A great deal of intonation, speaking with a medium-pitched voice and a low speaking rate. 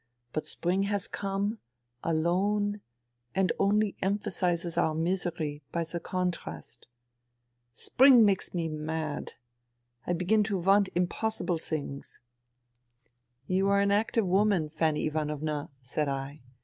No: average, 4.5 semitones; medium, 175 Hz; slow, 125 wpm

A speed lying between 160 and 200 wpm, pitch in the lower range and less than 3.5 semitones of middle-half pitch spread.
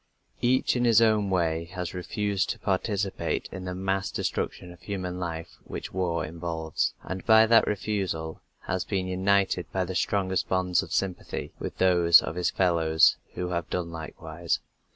Yes: average, 165 wpm; very low, 90 Hz; narrow, 2.4 semitones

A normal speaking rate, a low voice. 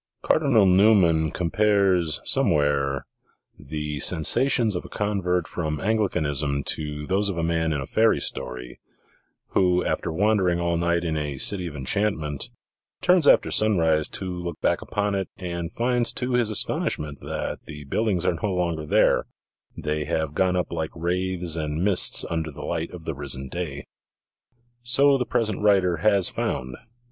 Yes: average, 160 wpm; very low, 85 Hz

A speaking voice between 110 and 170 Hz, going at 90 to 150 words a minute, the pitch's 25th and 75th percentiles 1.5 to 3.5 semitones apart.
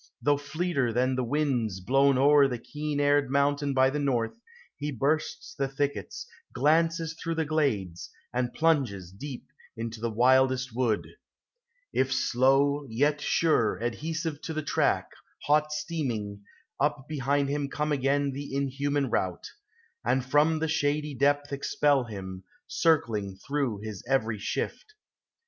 Yes: medium, 140 Hz; average, 140 wpm; average, 3.2 semitones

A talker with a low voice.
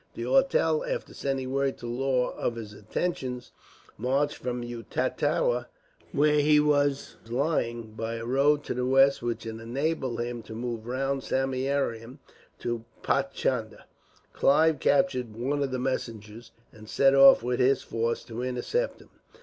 Yes: low, 130 Hz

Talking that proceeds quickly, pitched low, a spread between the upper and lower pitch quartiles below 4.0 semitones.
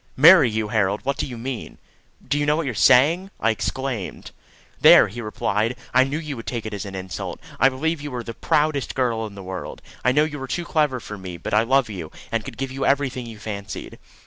No: fast, 240 wpm; low, 125 Hz; average, 4.6 semitones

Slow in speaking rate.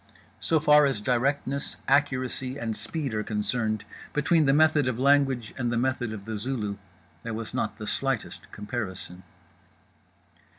No: average, 145 wpm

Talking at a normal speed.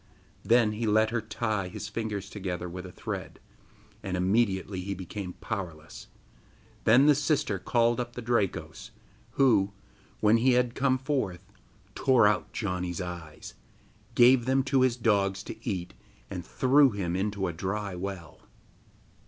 Yes: average, 145 wpm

